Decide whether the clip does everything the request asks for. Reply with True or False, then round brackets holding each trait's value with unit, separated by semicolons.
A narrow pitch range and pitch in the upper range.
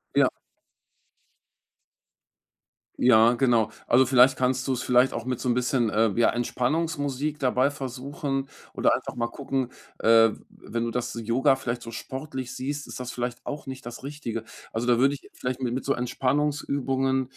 False (2.1 semitones; 130 Hz)